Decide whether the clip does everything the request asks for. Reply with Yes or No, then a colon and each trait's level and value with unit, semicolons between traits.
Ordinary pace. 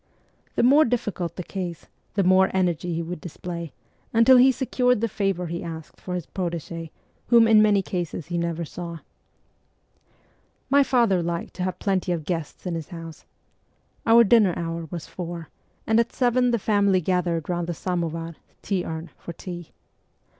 Yes: average, 175 wpm